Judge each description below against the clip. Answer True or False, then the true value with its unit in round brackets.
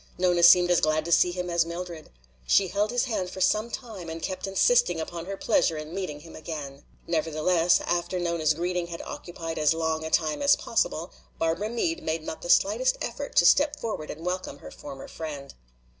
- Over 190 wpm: True (200 wpm)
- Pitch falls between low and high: True (170 Hz)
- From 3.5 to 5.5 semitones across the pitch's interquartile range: False (2.8 semitones)